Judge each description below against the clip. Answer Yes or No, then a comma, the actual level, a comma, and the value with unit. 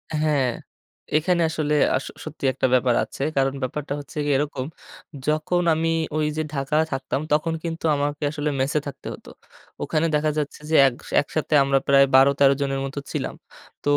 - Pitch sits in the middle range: Yes, medium, 145 Hz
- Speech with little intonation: Yes, narrow, 2.2 semitones